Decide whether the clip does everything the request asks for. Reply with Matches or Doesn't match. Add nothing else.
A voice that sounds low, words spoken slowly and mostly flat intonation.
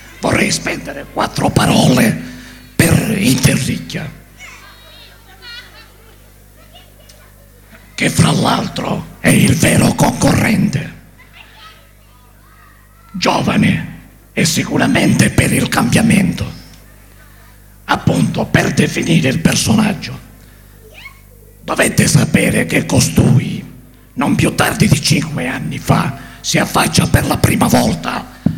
Matches